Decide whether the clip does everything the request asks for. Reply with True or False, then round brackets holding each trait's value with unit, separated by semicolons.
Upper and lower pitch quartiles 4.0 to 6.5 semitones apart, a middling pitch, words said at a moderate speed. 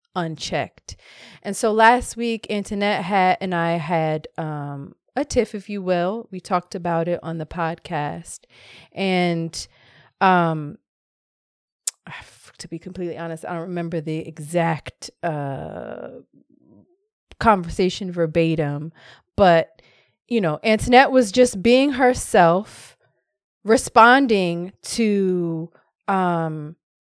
False (4.4 semitones; 175 Hz; 105 wpm)